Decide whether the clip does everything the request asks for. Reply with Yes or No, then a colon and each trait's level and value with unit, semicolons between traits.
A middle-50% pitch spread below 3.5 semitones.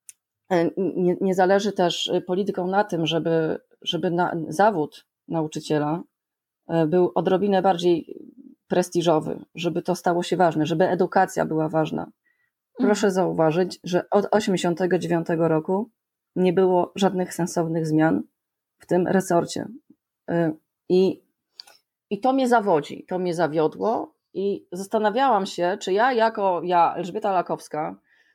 Yes: average, 2.7 semitones